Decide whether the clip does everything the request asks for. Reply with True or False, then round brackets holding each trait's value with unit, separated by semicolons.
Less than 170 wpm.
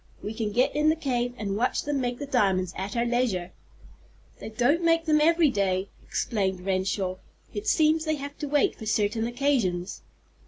False (185 wpm)